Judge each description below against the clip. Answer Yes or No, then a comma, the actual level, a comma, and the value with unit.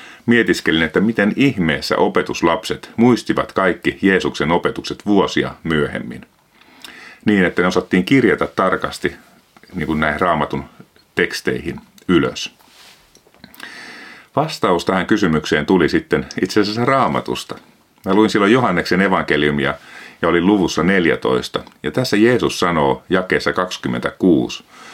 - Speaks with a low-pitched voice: Yes, very low, 95 Hz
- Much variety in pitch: Yes, wide, 7.2 semitones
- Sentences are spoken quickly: No, average, 110 wpm